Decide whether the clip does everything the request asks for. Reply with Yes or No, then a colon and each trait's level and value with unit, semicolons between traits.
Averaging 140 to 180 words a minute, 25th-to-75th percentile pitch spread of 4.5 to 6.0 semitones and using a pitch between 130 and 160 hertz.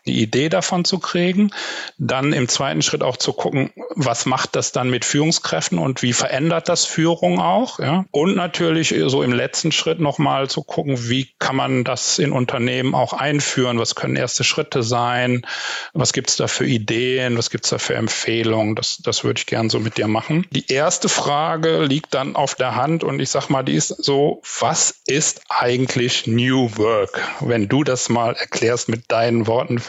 No: fast, 190 wpm; average, 5.0 semitones; low, 135 Hz